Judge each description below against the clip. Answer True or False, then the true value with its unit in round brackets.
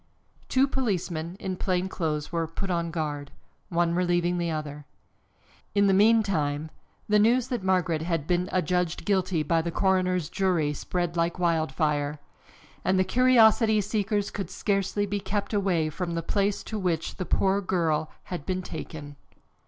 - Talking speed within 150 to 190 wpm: True (160 wpm)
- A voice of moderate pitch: True (180 Hz)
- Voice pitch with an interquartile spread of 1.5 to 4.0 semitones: True (3.4 semitones)